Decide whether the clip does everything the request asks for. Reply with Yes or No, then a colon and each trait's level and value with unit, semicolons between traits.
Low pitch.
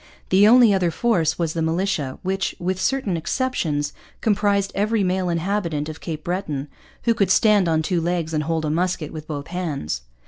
No: medium, 175 Hz